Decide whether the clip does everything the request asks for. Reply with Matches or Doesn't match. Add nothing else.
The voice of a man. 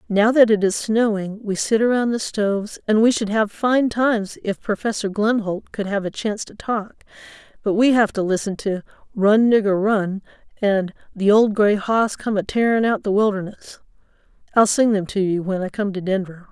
Doesn't match